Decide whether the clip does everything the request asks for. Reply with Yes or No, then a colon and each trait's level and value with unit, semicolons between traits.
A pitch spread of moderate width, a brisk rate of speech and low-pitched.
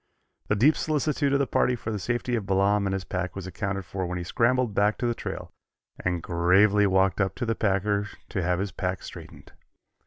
Yes: average, 3.5 semitones; fast, 215 wpm; low, 100 Hz